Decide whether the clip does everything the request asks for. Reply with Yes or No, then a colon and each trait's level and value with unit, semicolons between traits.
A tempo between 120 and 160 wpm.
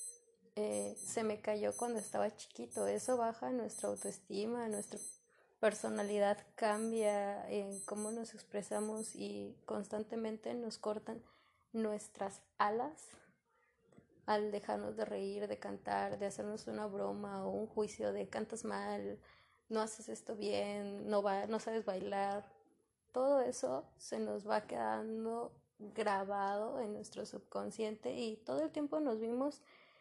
Yes: average, 130 wpm